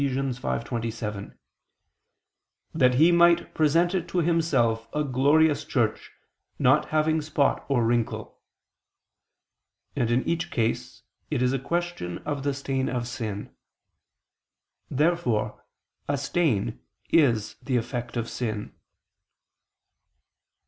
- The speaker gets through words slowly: Yes, slow, 105 wpm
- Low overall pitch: Yes, low, 130 Hz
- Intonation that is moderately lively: Yes, average, 4.9 semitones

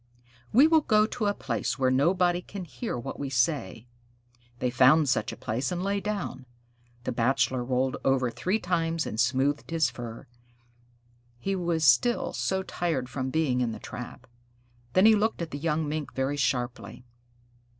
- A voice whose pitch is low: No, medium, 145 Hz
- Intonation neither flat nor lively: No, wide, 5.8 semitones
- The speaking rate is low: No, average, 170 wpm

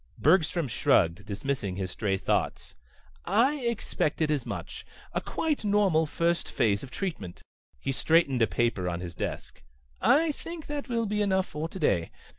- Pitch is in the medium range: Yes, medium, 155 Hz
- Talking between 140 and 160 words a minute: Yes, average, 155 wpm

